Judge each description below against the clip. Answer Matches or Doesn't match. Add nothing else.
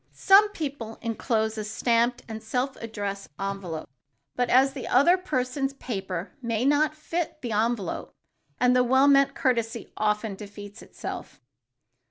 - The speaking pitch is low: Doesn't match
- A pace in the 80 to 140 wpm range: Matches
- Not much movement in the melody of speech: Doesn't match